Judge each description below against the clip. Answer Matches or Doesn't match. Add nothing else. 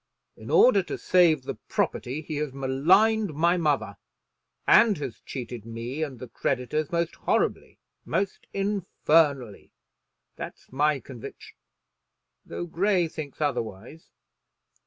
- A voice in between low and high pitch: Matches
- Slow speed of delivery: Matches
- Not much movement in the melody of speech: Doesn't match